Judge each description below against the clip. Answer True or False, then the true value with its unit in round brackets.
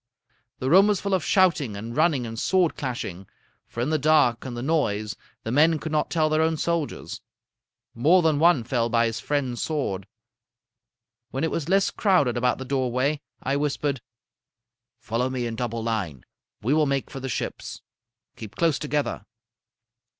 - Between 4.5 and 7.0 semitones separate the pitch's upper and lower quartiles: True (5.0 semitones)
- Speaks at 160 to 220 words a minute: True (170 wpm)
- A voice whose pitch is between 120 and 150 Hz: True (135 Hz)